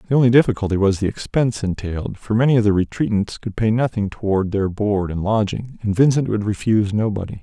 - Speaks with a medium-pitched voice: No, low, 105 Hz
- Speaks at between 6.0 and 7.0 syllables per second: Yes, 6.1 syllables/s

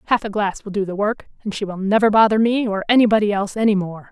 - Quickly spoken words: Yes, fast, 265 wpm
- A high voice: Yes, high, 210 Hz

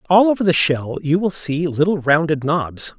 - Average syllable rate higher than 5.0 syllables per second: No, 4.7 syllables/s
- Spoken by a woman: No, male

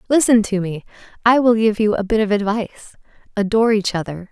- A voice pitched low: No, high, 210 Hz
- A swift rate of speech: No, average, 195 wpm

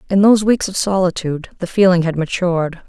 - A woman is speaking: Yes, female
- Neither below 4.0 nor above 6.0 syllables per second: No, 6.3 syllables/s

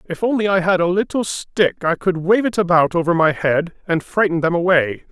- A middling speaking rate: No, fast, 225 wpm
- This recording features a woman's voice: No, male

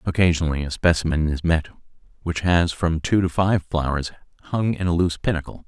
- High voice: No, very low, 85 Hz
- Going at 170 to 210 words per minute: Yes, average, 180 wpm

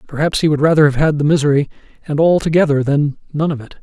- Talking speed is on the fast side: Yes, fast, 235 wpm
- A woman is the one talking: No, male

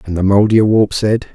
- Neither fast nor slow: Yes, average, 180 wpm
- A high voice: No, low, 105 Hz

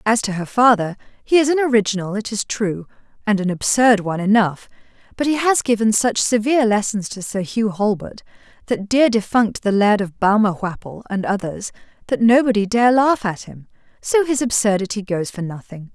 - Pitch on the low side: No, high, 215 Hz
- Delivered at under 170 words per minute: No, average, 180 wpm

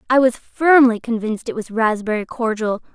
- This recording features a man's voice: No, female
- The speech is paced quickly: No, average, 165 wpm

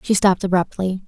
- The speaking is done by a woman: Yes, female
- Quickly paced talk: No, average, 170 wpm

